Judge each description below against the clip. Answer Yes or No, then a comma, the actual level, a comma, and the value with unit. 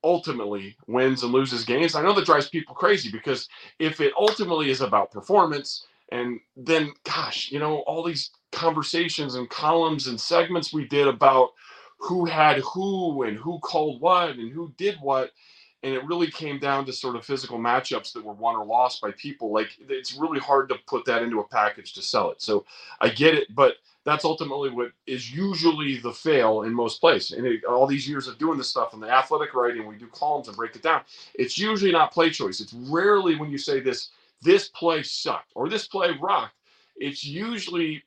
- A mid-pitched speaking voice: Yes, medium, 150 Hz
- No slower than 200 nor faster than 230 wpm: Yes, fast, 205 wpm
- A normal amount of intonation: Yes, average, 4.7 semitones